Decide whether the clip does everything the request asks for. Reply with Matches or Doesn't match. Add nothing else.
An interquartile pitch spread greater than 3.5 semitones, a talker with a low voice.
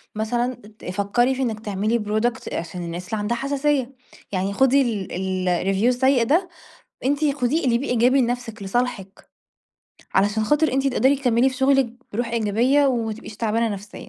Doesn't match